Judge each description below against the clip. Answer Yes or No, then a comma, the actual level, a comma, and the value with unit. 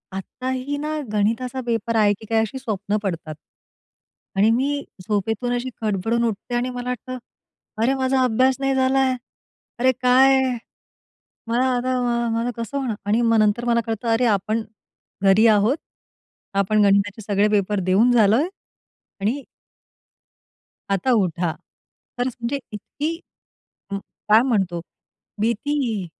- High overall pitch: Yes, high, 230 Hz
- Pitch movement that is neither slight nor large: Yes, average, 3.7 semitones